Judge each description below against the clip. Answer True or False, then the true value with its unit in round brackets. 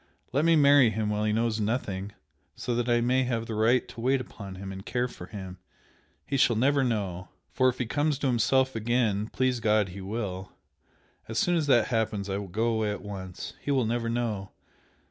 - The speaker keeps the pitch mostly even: False (3.7 semitones)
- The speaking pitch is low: True (115 Hz)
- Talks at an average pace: False (210 wpm)